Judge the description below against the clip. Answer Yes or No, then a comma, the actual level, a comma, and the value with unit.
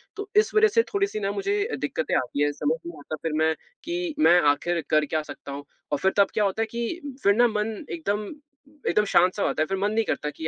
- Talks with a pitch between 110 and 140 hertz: No, high, 205 Hz